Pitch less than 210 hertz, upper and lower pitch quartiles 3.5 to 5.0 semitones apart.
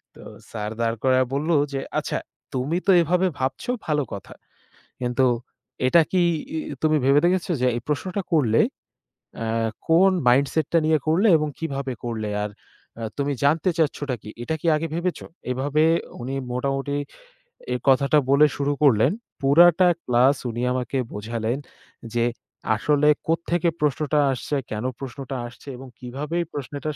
Yes: medium, 140 Hz; average, 3.9 semitones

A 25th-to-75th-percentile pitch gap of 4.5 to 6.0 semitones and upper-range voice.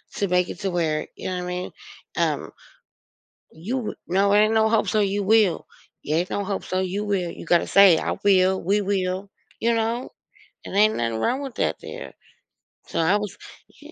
No: average, 2.9 semitones; high, 195 Hz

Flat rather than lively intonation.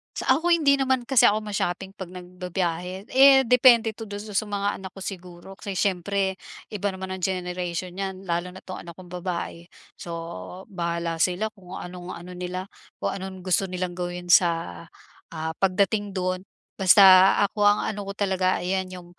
Yes: narrow, 2.1 semitones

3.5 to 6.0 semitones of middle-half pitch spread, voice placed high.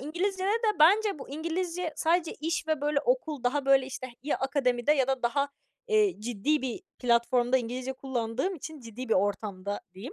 Yes: average, 5.2 semitones; very high, 275 Hz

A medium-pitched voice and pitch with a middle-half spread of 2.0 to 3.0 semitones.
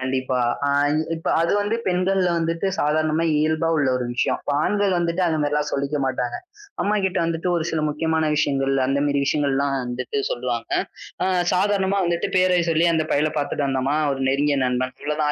No: medium, 150 Hz; average, 3.5 semitones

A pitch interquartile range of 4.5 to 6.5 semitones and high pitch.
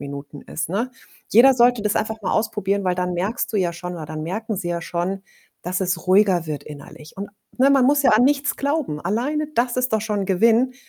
Yes: wide, 5.5 semitones; high, 200 Hz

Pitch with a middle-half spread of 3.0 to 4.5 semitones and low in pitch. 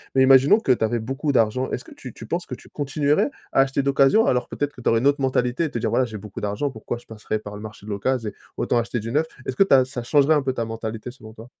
Yes: average, 3.6 semitones; low, 125 Hz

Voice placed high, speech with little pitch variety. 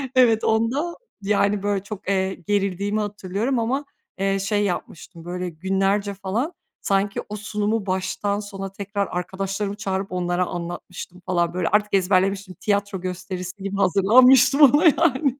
Yes: high, 200 Hz; narrow, 2.1 semitones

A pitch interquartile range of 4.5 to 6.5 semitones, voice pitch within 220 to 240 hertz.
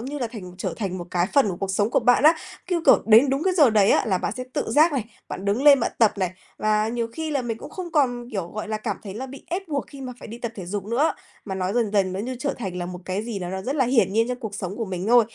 Yes: average, 5.2 semitones; high, 225 Hz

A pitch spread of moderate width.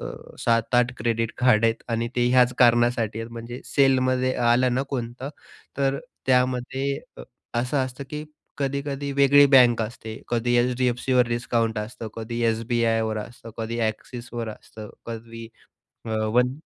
No: narrow, 2.0 semitones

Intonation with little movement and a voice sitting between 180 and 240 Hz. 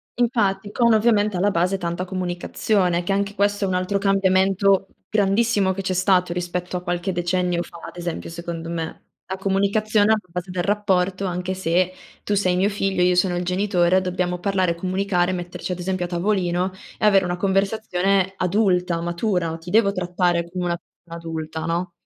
Yes: narrow, 1.9 semitones; medium, 185 Hz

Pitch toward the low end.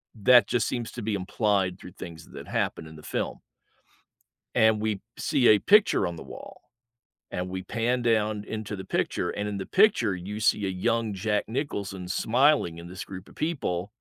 Yes: low, 105 Hz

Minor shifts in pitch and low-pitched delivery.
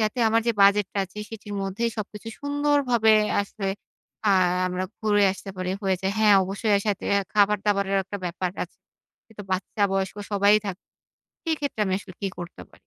No: narrow, 2.1 semitones; high, 205 Hz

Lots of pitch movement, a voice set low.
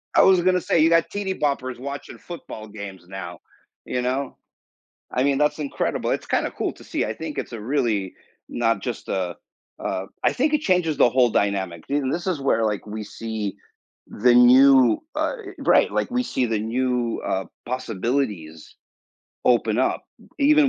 Yes: wide, 5.7 semitones; low, 125 Hz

